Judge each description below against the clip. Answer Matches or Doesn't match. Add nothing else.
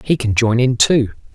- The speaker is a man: Matches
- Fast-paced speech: Matches